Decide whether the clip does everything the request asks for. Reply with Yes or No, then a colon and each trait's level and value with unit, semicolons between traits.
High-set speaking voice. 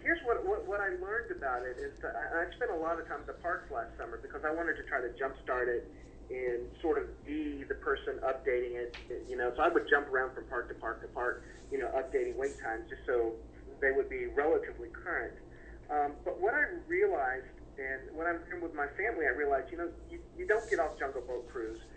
Yes: very high, 350 Hz